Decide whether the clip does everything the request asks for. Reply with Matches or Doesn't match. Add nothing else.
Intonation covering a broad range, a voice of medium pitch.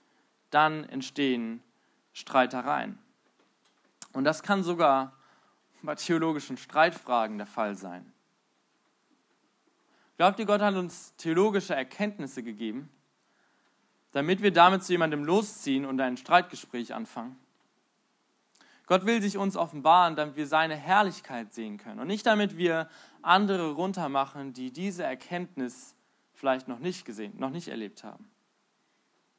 Matches